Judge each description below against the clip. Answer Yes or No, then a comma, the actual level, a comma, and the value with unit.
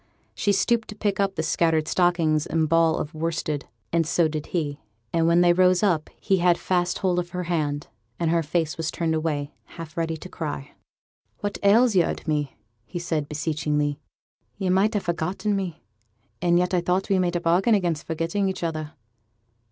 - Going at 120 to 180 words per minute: No, average, 190 wpm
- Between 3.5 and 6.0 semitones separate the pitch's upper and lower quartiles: No, average, 2.7 semitones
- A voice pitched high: No, medium, 170 Hz